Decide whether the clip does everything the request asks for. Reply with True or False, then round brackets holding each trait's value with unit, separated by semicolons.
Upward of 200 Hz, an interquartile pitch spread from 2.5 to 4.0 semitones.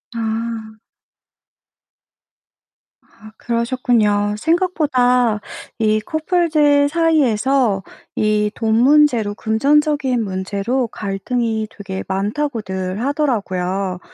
False (230 Hz; 5.2 semitones)